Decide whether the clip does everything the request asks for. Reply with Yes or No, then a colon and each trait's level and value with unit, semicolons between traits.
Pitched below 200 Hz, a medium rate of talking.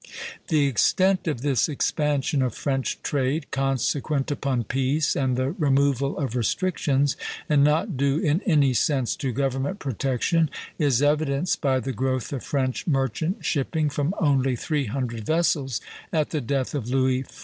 Yes: medium, 140 Hz; average, 155 wpm